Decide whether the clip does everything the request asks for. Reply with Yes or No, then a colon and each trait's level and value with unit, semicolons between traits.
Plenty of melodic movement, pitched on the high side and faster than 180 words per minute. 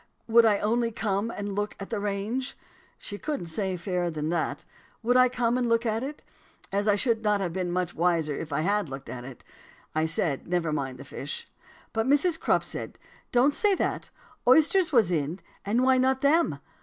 Yes: wide, 6.1 semitones; high, 205 Hz; average, 200 wpm